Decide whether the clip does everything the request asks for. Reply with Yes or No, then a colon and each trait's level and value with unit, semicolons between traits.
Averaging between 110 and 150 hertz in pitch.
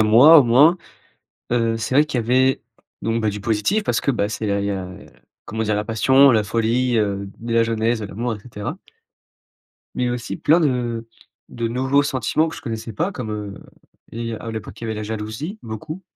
Yes: low, 115 Hz